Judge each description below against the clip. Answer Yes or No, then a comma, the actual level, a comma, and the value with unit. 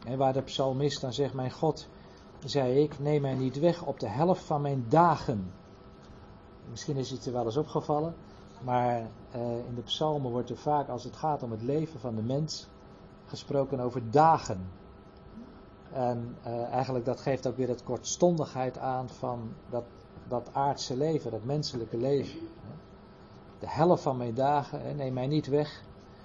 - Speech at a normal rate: Yes, average, 165 wpm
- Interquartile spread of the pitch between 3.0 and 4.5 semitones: Yes, average, 3.6 semitones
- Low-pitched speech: Yes, low, 130 Hz